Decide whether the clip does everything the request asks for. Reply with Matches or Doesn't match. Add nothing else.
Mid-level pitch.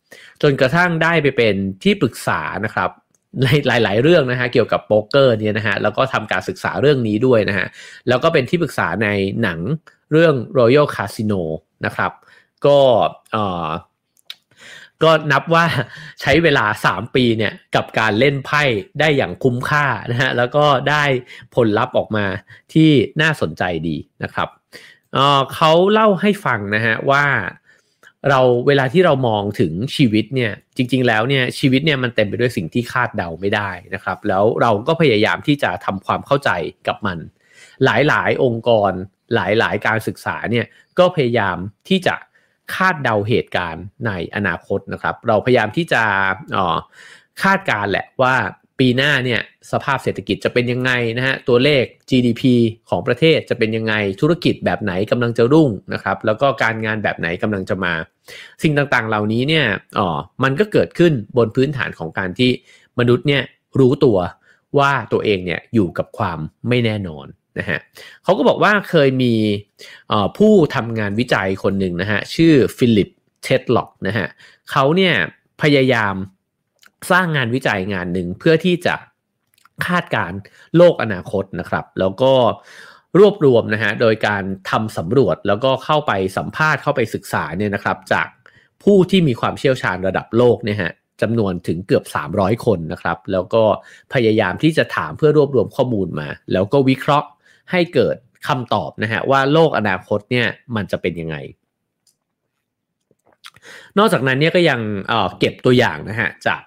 Doesn't match